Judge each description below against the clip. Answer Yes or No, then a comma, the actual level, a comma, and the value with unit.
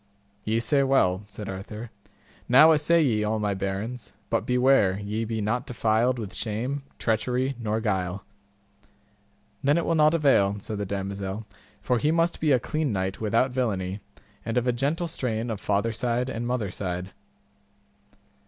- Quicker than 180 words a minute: No, average, 160 wpm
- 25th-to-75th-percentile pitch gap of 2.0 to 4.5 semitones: Yes, average, 4.2 semitones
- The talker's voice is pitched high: No, low, 115 Hz